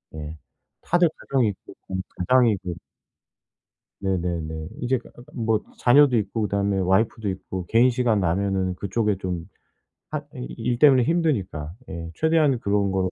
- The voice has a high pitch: No, low, 100 Hz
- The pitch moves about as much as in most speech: Yes, average, 4.9 semitones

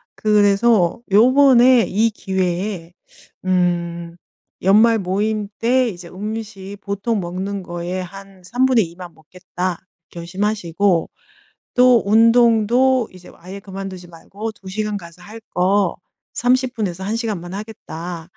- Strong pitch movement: No, average, 3.8 semitones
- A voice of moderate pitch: No, high, 200 Hz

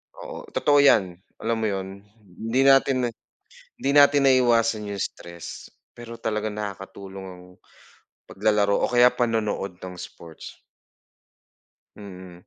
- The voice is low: Yes, low, 105 Hz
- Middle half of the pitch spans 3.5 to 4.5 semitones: Yes, average, 3.8 semitones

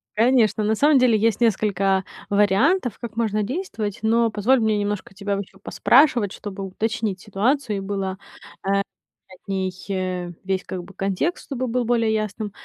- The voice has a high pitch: Yes, high, 210 Hz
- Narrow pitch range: No, average, 3.1 semitones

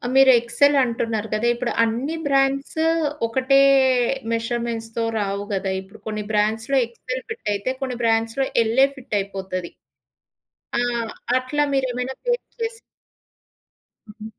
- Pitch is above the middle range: Yes, high, 235 Hz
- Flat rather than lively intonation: No, average, 3.6 semitones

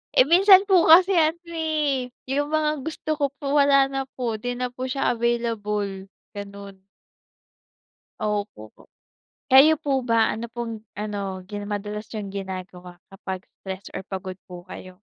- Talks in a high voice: Yes, high, 230 Hz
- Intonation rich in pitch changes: Yes, wide, 6.0 semitones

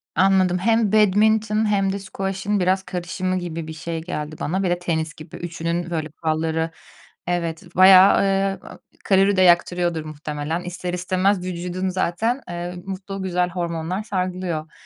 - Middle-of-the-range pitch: Yes, medium, 180 Hz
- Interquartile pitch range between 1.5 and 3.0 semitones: Yes, narrow, 2.4 semitones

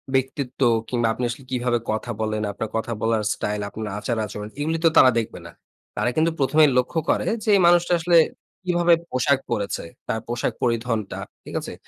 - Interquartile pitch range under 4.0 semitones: No, average, 4.6 semitones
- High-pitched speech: No, low, 125 Hz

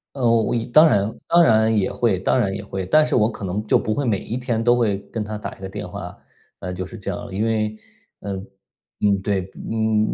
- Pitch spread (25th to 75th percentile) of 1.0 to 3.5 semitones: Yes, average, 2.8 semitones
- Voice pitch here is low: Yes, low, 110 Hz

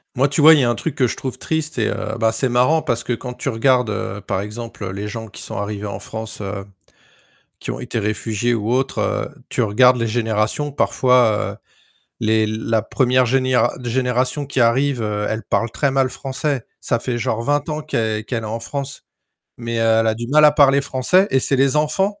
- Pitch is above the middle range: No, low, 120 Hz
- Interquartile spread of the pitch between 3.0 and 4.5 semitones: Yes, average, 3.5 semitones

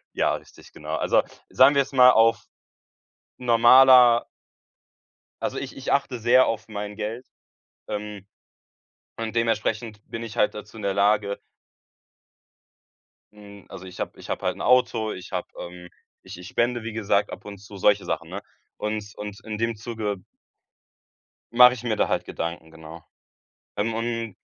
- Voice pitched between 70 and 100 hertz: No, low, 110 Hz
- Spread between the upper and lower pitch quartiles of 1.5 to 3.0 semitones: Yes, average, 2.7 semitones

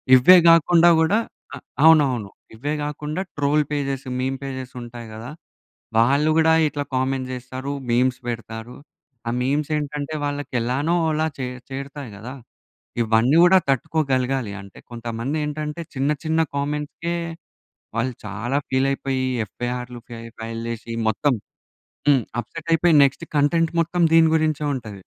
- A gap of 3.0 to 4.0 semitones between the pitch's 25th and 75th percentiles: Yes, average, 3.6 semitones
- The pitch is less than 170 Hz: Yes, low, 135 Hz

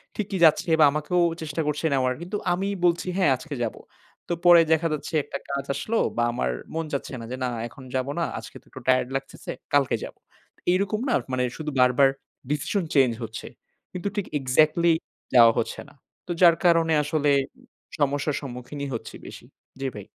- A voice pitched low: No, medium, 150 Hz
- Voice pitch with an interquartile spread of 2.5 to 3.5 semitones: No, average, 4.7 semitones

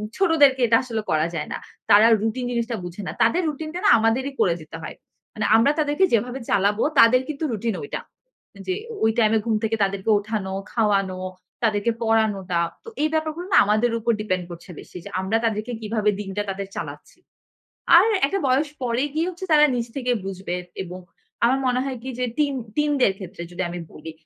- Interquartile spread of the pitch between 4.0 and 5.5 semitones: Yes, average, 5.0 semitones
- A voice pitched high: Yes, high, 225 Hz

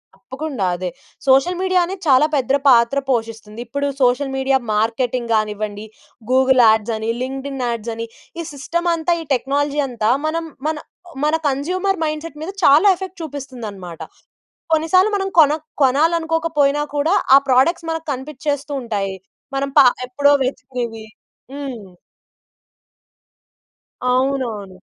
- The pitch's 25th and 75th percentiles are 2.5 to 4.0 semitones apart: No, average, 4.9 semitones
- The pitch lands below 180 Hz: No, very high, 270 Hz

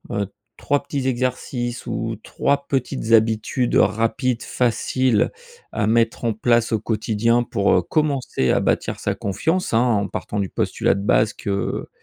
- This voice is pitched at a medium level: No, low, 115 Hz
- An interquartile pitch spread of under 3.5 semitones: Yes, average, 2.9 semitones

